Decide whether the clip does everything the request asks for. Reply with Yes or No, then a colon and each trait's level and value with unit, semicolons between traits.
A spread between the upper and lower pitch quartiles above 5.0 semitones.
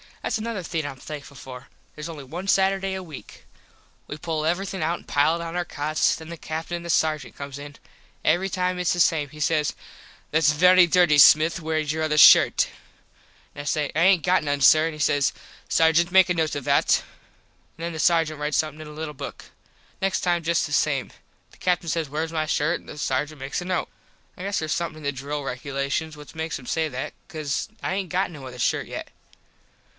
No: average, 2.8 semitones